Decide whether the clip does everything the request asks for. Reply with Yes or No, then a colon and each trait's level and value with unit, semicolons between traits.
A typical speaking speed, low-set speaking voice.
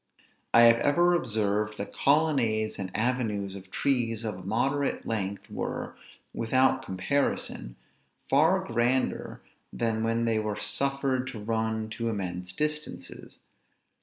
No: slow, 125 wpm; low, 115 Hz